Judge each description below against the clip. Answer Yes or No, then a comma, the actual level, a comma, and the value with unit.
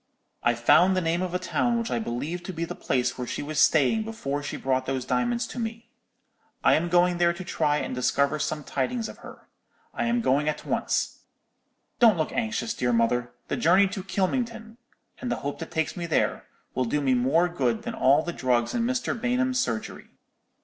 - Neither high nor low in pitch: Yes, medium, 170 Hz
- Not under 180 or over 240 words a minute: Yes, fast, 205 wpm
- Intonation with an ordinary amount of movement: No, wide, 8.8 semitones